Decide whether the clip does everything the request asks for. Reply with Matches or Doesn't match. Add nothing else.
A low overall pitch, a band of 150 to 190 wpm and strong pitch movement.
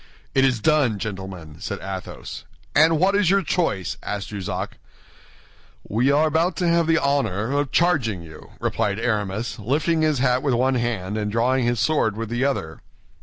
Matches